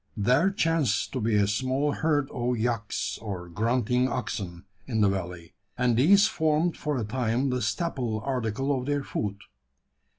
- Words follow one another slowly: No, average, 160 wpm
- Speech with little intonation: No, average, 4.7 semitones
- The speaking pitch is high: No, low, 125 Hz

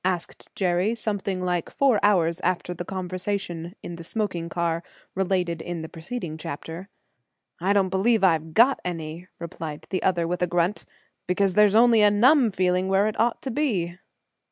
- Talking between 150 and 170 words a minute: Yes, average, 165 wpm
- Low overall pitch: No, medium, 185 Hz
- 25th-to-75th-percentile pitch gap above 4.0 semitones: No, average, 3.3 semitones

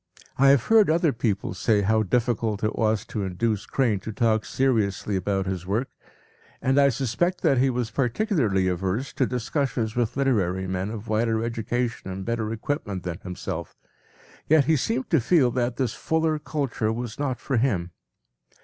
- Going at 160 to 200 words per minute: Yes, average, 175 wpm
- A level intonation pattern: No, average, 4.6 semitones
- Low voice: Yes, low, 115 Hz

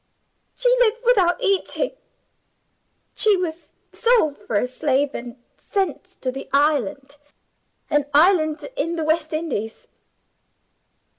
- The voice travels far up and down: Yes, wide, 5.9 semitones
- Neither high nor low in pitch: No, very high, 315 Hz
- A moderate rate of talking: No, slow, 115 wpm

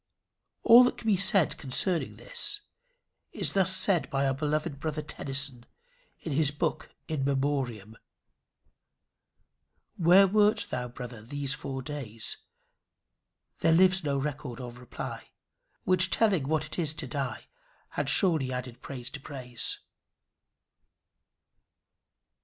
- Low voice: No, medium, 145 Hz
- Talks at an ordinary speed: No, slow, 125 wpm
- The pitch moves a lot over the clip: No, average, 4.9 semitones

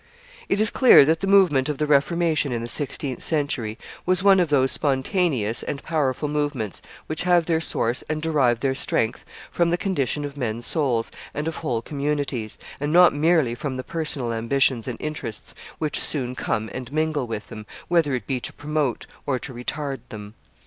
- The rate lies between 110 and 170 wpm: No, average, 190 wpm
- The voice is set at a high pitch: No, medium, 145 Hz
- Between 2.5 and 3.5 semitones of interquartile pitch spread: No, average, 4.3 semitones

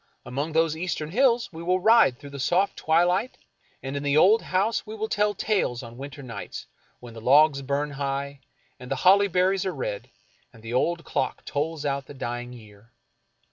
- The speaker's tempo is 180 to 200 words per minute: Yes, average, 190 wpm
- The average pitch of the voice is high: No, medium, 150 Hz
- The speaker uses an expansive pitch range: Yes, wide, 5.7 semitones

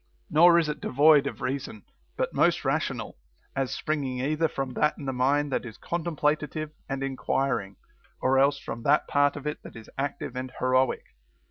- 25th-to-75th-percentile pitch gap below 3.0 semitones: Yes, narrow, 2.6 semitones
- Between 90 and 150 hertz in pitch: Yes, medium, 140 Hz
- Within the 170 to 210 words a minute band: Yes, average, 175 wpm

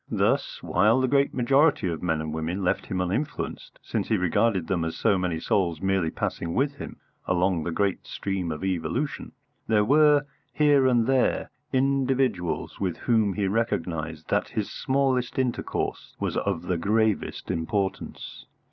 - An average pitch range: No, wide, 6.6 semitones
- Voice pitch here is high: No, low, 100 Hz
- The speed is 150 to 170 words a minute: Yes, average, 155 wpm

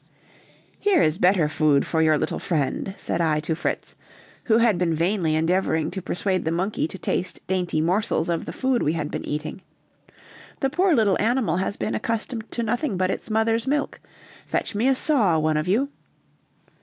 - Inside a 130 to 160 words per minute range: No, average, 185 wpm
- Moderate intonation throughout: No, wide, 6.0 semitones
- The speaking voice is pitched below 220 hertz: Yes, medium, 185 Hz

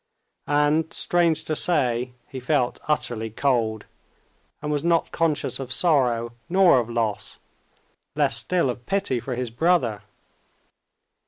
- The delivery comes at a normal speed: No, slow, 130 wpm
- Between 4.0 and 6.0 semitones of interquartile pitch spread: Yes, average, 5.2 semitones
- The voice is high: No, low, 135 Hz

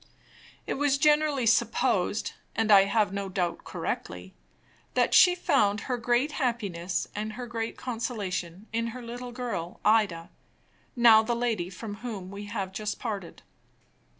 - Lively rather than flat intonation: No, average, 3.6 semitones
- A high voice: Yes, high, 225 Hz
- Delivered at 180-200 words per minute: No, average, 145 wpm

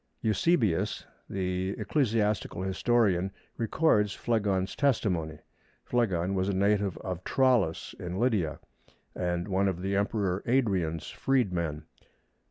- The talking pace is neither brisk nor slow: No, slow, 105 wpm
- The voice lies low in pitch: Yes, low, 100 Hz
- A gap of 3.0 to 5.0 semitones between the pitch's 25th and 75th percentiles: Yes, average, 3.6 semitones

